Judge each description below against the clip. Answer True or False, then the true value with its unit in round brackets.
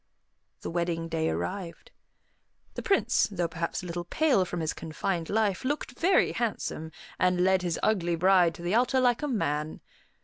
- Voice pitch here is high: False (180 Hz)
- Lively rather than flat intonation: False (4.8 semitones)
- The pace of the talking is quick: False (170 wpm)